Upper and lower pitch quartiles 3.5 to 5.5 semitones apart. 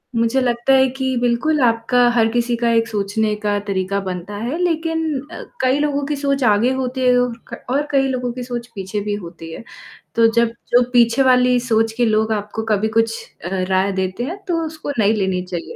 Yes: average, 3.8 semitones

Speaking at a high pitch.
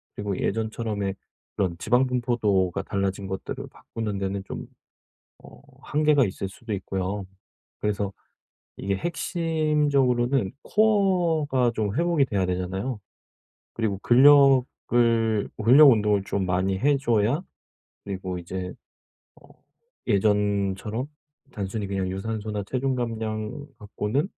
No: low, 110 Hz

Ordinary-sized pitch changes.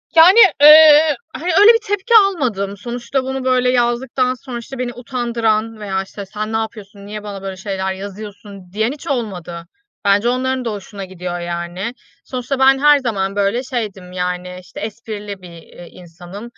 Yes: average, 4.9 semitones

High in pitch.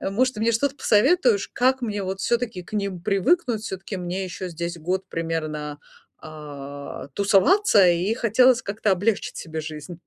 Yes: high, 195 Hz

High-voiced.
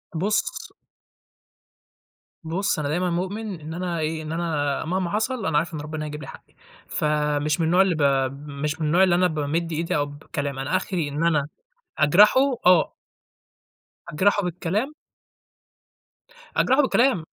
No: medium, 165 Hz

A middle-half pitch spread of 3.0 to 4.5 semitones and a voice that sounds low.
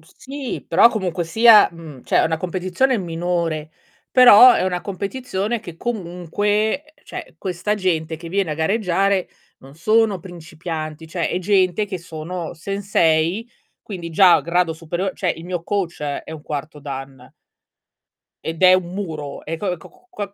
No: average, 3.7 semitones; medium, 180 Hz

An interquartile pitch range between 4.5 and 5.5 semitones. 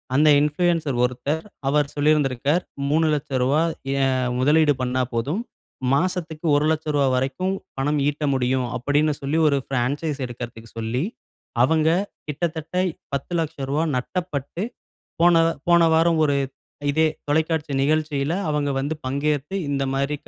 No: average, 2.8 semitones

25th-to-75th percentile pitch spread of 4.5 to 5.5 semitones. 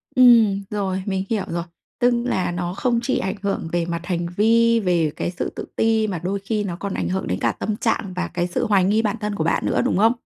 No: average, 3.7 semitones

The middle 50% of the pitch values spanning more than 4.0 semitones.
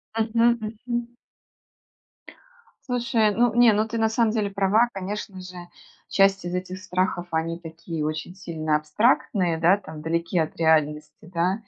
Yes: average, 4.9 semitones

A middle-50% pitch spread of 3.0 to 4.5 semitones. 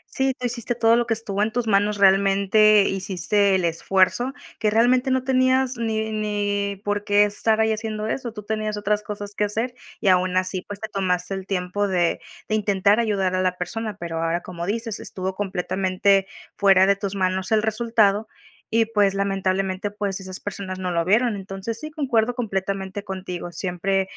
No: narrow, 2.6 semitones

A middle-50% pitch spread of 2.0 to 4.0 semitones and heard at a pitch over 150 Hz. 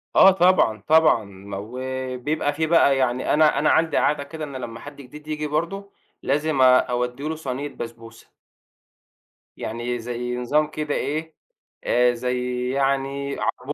No: average, 3.7 semitones; low, 135 Hz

